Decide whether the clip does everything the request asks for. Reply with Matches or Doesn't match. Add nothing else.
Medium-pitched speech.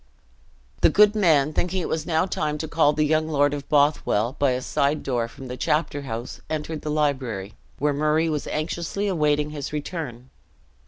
Matches